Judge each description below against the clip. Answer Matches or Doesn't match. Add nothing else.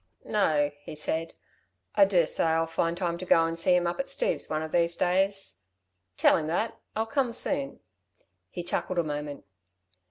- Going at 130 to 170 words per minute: Doesn't match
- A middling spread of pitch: Matches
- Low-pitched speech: Doesn't match